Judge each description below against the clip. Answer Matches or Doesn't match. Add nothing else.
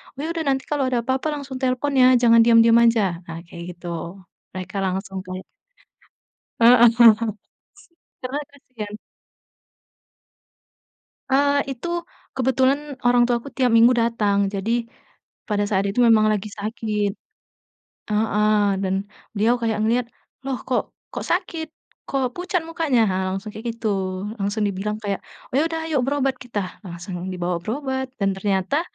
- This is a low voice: Doesn't match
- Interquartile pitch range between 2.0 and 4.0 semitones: Doesn't match